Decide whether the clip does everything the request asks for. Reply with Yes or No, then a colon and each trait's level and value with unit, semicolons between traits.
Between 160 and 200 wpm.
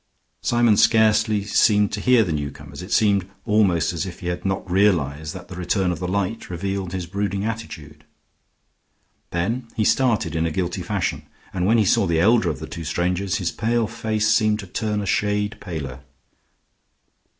Yes: average, 180 wpm